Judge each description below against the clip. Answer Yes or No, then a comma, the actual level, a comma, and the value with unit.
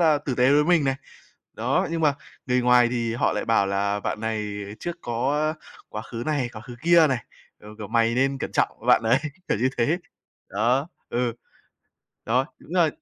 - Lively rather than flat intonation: No, average, 4.3 semitones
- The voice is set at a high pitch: No, low, 125 Hz